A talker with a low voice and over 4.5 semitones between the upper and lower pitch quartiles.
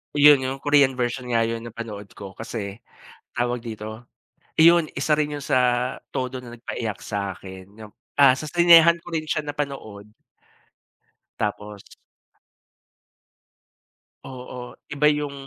Yes: low, 125 Hz; average, 5.0 semitones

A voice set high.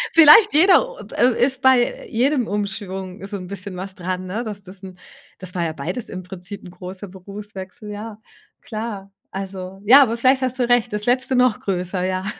Yes: high, 205 Hz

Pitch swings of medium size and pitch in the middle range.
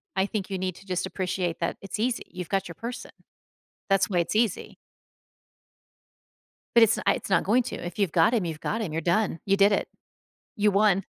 No: average, 3.0 semitones; high, 195 Hz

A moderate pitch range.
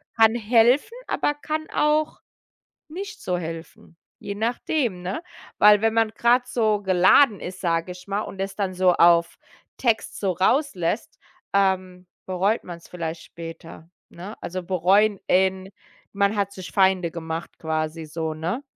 Yes: average, 4.3 semitones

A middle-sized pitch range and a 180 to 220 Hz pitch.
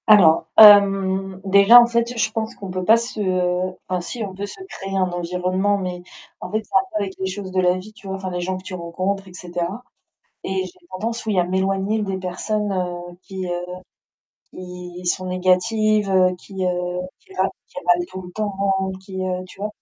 No: narrow, 2.0 semitones; high, 190 Hz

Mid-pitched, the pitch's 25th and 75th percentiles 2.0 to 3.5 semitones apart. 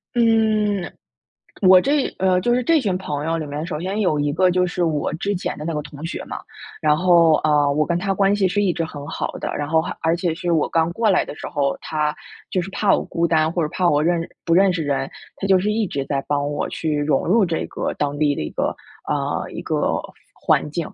No: medium, 170 Hz; average, 4.0 semitones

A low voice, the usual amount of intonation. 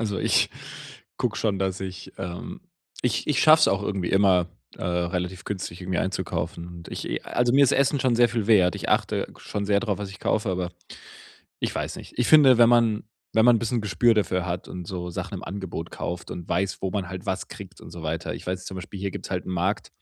Yes: very low, 95 Hz; average, 3.9 semitones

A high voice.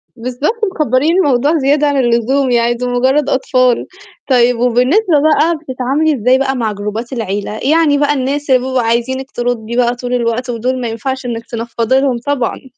Yes: very high, 255 Hz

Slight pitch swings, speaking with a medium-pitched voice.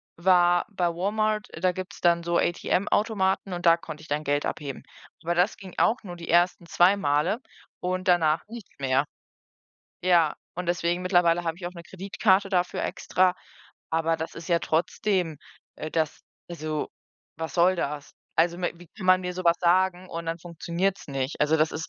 Yes: narrow, 2.1 semitones; medium, 175 Hz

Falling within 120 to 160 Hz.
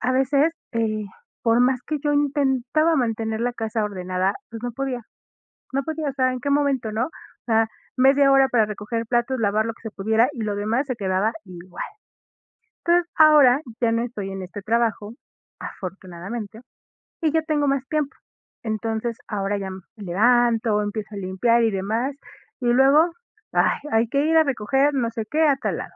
No: high, 235 Hz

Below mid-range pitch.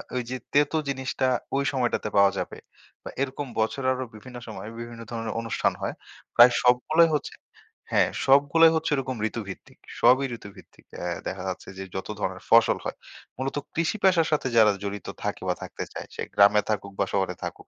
Yes: low, 125 Hz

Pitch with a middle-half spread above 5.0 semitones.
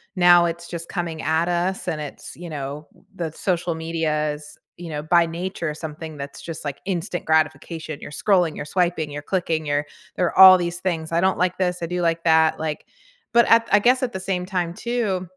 No: narrow, 2.4 semitones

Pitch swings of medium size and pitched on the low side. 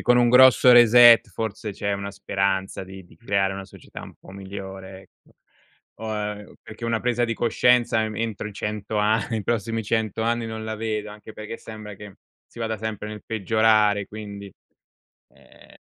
No: narrow, 2.0 semitones; low, 110 Hz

